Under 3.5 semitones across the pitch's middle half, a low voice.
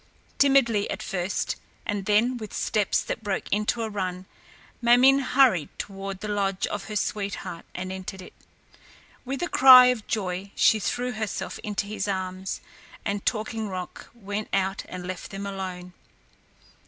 No: average, 2.8 semitones; high, 205 Hz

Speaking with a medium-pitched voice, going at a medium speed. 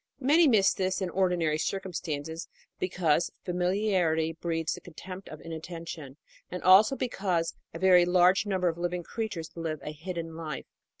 Yes: medium, 175 Hz; average, 155 wpm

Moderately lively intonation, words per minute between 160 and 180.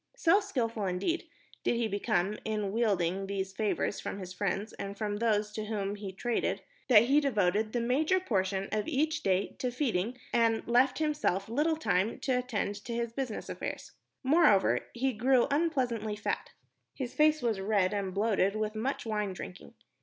Yes: average, 4.3 semitones; average, 170 wpm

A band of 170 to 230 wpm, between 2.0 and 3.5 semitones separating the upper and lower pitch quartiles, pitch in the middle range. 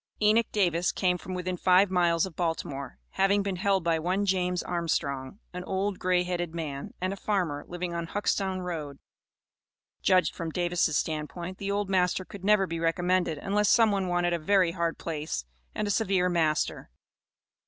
Yes: average, 175 wpm; narrow, 2.5 semitones; medium, 180 Hz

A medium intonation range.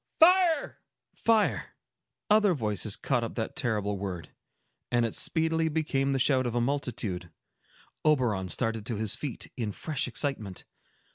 No: wide, 6.2 semitones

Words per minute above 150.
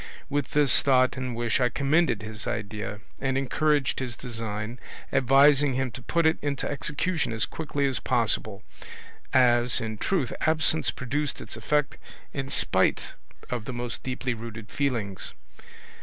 No: average, 145 wpm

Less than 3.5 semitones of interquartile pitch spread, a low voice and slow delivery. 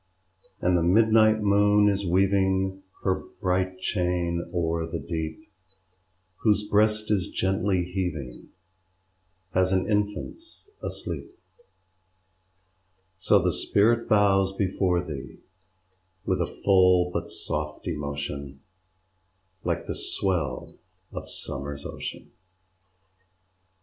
Yes: average, 3.1 semitones; very low, 95 Hz; slow, 100 wpm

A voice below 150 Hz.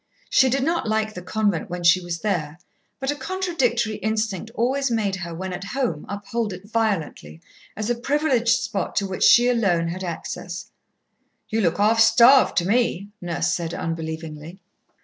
No: high, 210 Hz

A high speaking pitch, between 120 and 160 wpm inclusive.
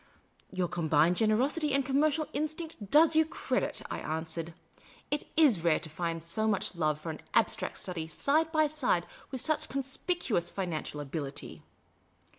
Yes: high, 205 Hz; average, 155 wpm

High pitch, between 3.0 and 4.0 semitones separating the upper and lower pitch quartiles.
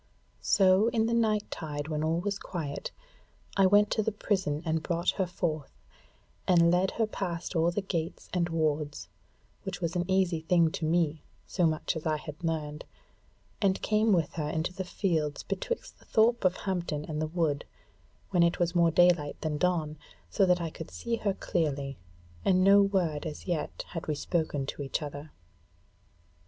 No: medium, 170 Hz; average, 3.5 semitones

